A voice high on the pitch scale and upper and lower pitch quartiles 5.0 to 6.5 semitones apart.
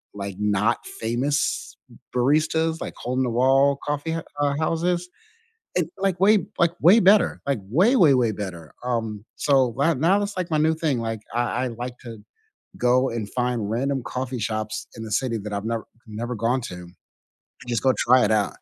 No: low, 125 Hz; wide, 5.6 semitones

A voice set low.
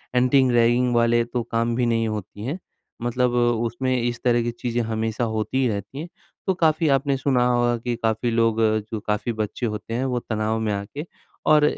Yes: low, 120 Hz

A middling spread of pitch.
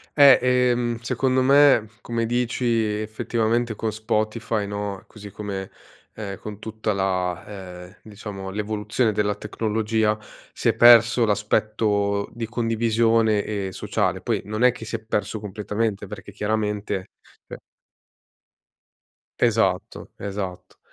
No: narrow, 2.0 semitones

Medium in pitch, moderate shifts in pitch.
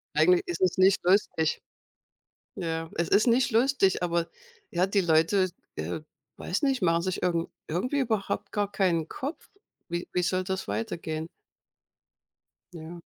Yes: medium, 180 Hz; average, 3.6 semitones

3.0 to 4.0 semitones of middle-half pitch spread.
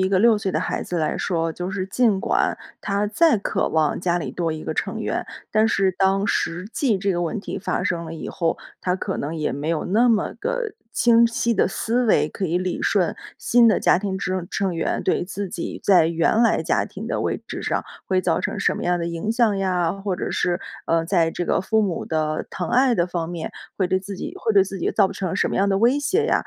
Yes: average, 3.7 semitones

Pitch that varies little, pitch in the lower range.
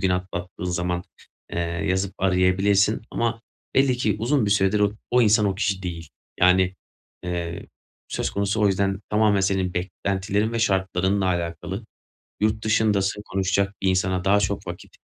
Yes: narrow, 2.1 semitones; very low, 95 Hz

